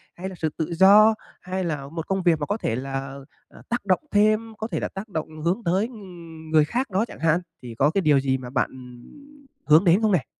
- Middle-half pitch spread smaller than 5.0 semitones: No, wide, 5.4 semitones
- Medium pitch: Yes, medium, 170 Hz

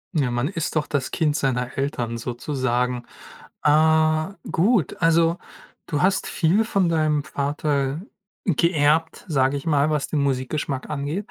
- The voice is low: No, medium, 150 Hz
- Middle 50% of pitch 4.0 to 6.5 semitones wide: No, average, 3.1 semitones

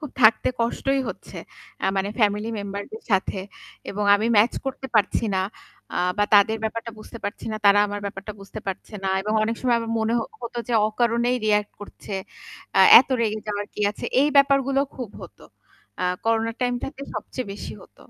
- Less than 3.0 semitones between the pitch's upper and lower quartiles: Yes, narrow, 2.6 semitones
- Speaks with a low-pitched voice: No, high, 220 Hz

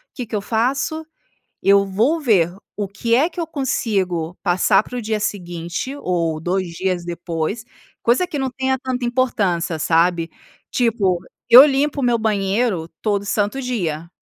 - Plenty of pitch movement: Yes, wide, 6.2 semitones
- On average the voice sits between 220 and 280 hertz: No, high, 210 Hz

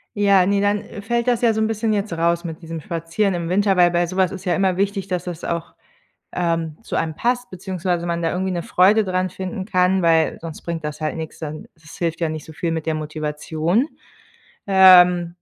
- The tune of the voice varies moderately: Yes, average, 3.0 semitones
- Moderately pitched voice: Yes, medium, 180 Hz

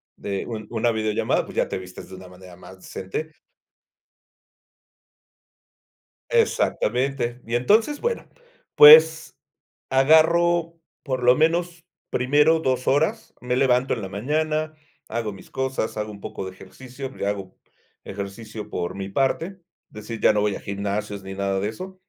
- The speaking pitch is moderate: No, low, 120 Hz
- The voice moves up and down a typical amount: No, wide, 7.5 semitones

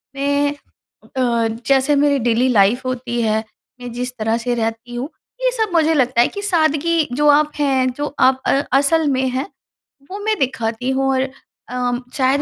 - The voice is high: Yes, very high, 260 Hz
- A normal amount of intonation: Yes, average, 3.2 semitones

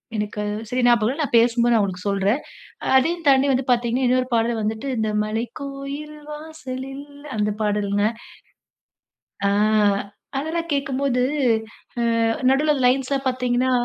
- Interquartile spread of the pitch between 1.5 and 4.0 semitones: Yes, average, 3.7 semitones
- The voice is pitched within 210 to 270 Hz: Yes, very high, 250 Hz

